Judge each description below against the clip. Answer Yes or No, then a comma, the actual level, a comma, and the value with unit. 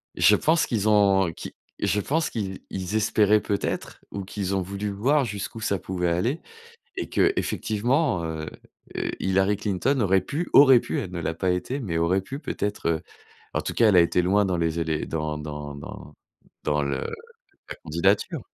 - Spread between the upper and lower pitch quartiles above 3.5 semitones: Yes, average, 4.3 semitones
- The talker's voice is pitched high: No, very low, 95 Hz